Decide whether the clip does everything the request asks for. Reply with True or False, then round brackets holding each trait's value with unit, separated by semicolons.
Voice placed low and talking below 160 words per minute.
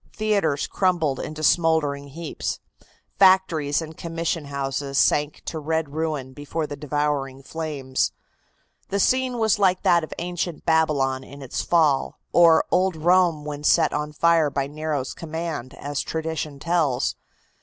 False (155 Hz; 140 wpm)